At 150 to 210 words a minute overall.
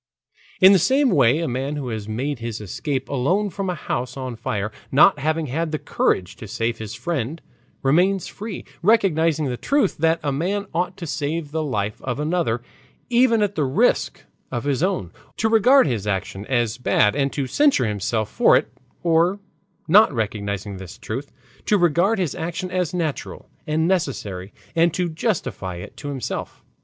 Yes: average, 175 wpm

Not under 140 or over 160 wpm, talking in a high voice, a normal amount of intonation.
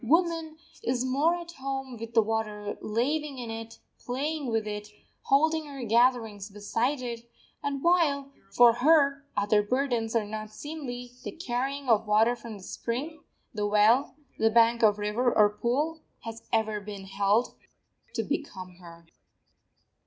Yes: average, 150 wpm; high, 235 Hz; average, 4.5 semitones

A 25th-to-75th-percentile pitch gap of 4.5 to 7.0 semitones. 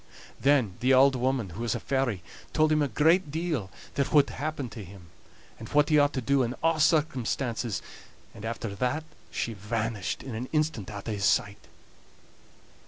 Yes: average, 5.1 semitones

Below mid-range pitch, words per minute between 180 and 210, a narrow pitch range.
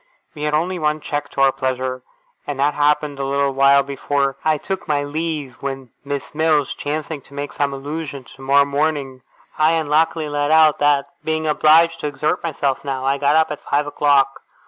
No: medium, 145 Hz; average, 190 wpm; narrow, 1.8 semitones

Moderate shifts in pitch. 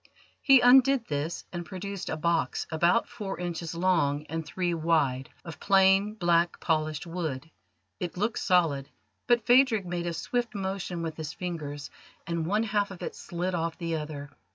Yes: average, 3.5 semitones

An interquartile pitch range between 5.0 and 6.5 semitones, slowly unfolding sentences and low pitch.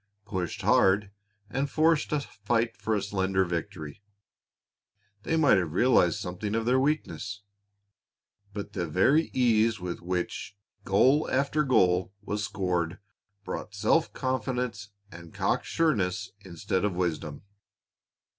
Yes: wide, 5.6 semitones; slow, 125 wpm; low, 100 Hz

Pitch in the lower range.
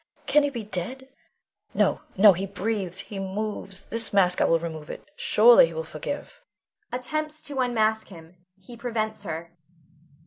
No: high, 215 Hz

